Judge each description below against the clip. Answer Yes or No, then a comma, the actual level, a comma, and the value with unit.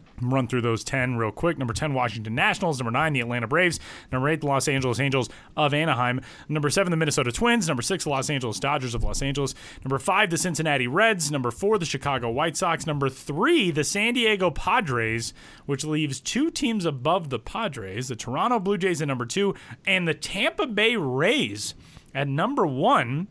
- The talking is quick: No, average, 195 wpm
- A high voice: No, medium, 140 Hz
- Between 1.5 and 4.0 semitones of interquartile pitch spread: No, average, 5.0 semitones